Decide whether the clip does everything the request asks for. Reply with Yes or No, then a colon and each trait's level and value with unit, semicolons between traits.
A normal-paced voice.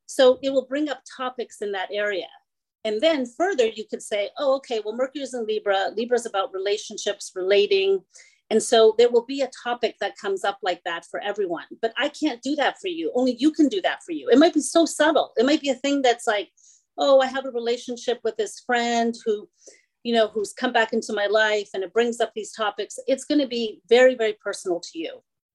No: fast, 230 wpm